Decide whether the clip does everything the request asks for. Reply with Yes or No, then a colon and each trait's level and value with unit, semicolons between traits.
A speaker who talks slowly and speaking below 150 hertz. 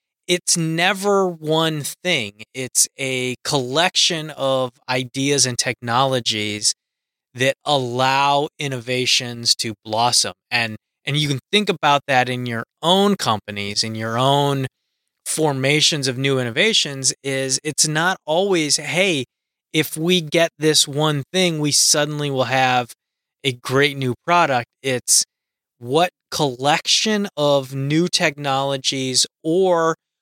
Yes: slow, 120 wpm; medium, 140 Hz